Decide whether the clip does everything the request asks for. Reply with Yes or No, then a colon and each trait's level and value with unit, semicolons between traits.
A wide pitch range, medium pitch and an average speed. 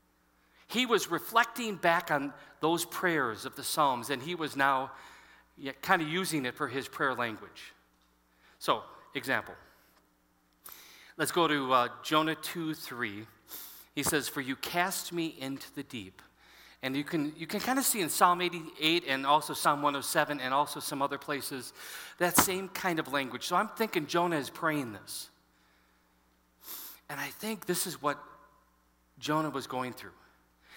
Yes: wide, 5.7 semitones; medium, 145 Hz; average, 160 wpm